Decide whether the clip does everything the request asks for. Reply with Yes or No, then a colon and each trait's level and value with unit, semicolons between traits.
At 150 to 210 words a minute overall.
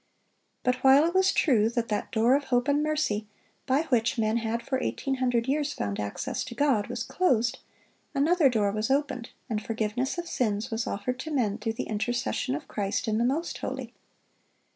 Yes: average, 190 wpm